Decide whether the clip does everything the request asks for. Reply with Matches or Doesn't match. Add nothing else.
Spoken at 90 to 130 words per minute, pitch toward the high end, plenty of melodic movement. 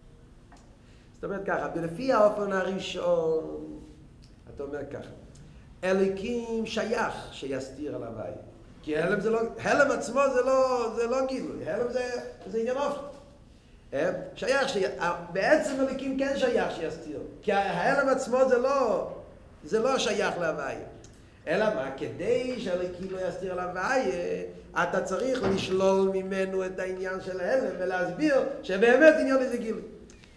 Matches